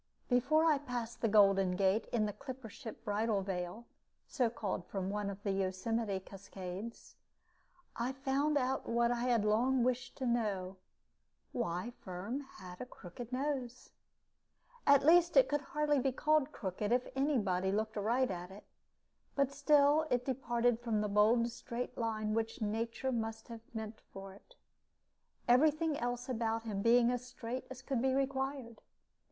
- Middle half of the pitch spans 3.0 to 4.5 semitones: Yes, average, 4.1 semitones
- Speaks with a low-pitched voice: No, high, 235 Hz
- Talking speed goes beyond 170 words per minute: No, average, 160 wpm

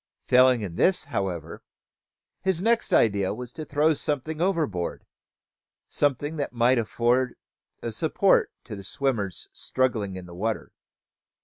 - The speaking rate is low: Yes, slow, 130 wpm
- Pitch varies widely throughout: Yes, wide, 6.7 semitones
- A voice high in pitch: No, low, 125 Hz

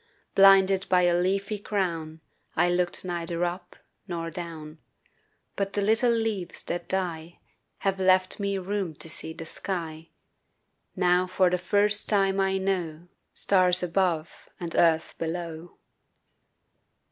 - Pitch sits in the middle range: Yes, medium, 180 Hz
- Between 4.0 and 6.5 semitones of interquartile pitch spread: No, narrow, 2.5 semitones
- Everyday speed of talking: No, slow, 130 wpm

